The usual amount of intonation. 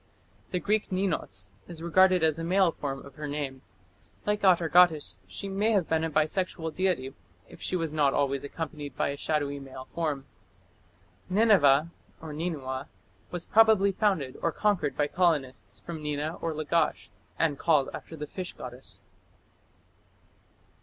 Yes: average, 4.2 semitones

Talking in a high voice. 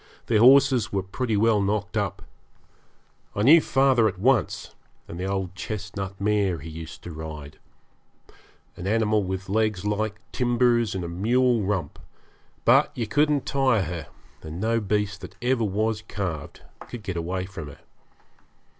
No: low, 105 Hz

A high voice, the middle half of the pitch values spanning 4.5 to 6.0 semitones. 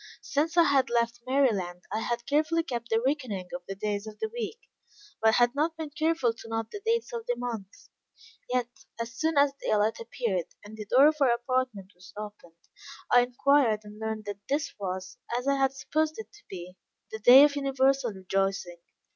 Yes: high, 240 Hz; average, 5.2 semitones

